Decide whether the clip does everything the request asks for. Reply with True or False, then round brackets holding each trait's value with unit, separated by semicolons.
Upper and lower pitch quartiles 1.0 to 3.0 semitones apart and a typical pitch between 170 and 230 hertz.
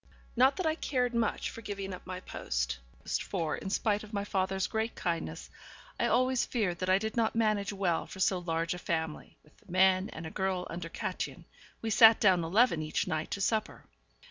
False (4.2 semitones; 190 Hz)